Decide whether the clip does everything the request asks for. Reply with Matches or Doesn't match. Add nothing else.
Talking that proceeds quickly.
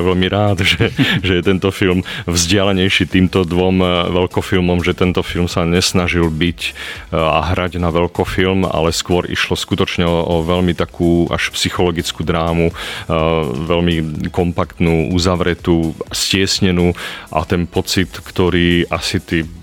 Doesn't match